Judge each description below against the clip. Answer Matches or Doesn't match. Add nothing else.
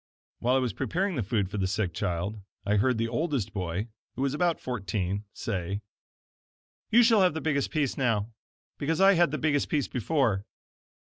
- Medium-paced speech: Matches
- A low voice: Matches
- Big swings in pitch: Matches